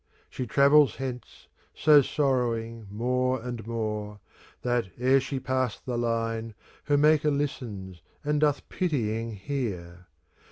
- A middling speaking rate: No, slow, 120 wpm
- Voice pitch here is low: Yes, low, 125 Hz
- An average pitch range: Yes, average, 3.7 semitones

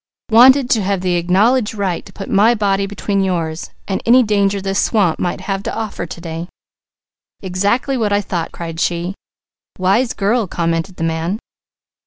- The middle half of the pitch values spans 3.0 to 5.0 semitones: Yes, average, 3.4 semitones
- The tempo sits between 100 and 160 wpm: No, average, 170 wpm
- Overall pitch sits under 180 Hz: No, high, 195 Hz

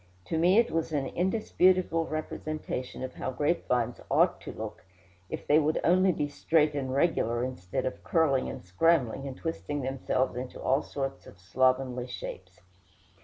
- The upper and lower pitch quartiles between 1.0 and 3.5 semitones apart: No, average, 4.2 semitones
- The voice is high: No, medium, 140 Hz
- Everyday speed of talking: Yes, average, 160 wpm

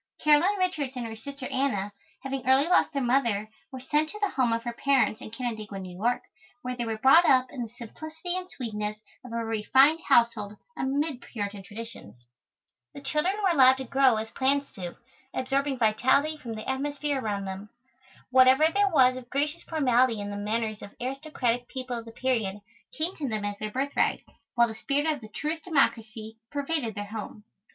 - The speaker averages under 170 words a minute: No, average, 190 wpm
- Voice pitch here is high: Yes, very high, 255 Hz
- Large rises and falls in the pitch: No, average, 4.3 semitones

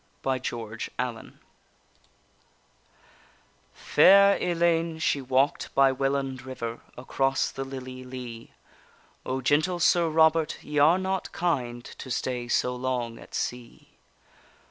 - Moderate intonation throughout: Yes, average, 4.3 semitones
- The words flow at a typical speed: No, slow, 115 wpm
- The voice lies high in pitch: No, low, 135 Hz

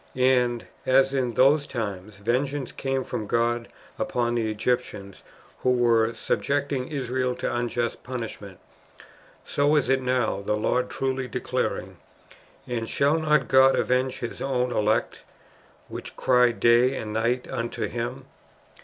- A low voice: Yes, low, 125 Hz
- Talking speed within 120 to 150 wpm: Yes, average, 140 wpm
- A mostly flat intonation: Yes, narrow, 2.2 semitones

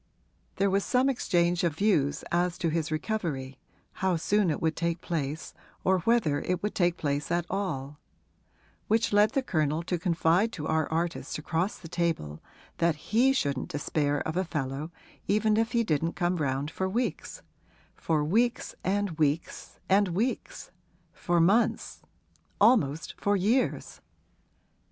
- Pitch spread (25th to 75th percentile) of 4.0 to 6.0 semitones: Yes, average, 4.8 semitones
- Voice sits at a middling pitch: Yes, medium, 170 Hz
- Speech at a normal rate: Yes, average, 150 wpm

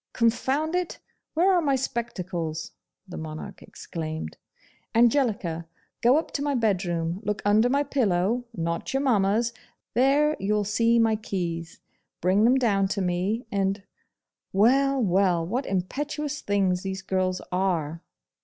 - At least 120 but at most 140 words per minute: Yes, slow, 135 wpm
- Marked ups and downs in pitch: Yes, wide, 5.7 semitones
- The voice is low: No, high, 205 Hz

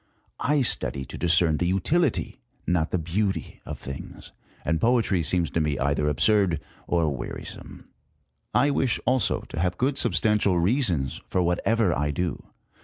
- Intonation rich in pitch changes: Yes, wide, 5.8 semitones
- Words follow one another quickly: No, average, 150 wpm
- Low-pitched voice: Yes, very low, 90 Hz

